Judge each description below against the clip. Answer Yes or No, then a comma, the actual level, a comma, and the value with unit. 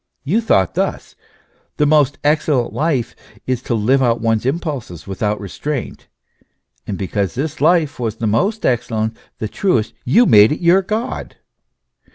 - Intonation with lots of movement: Yes, wide, 6.0 semitones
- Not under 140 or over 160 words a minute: Yes, average, 150 wpm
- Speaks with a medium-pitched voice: No, low, 130 Hz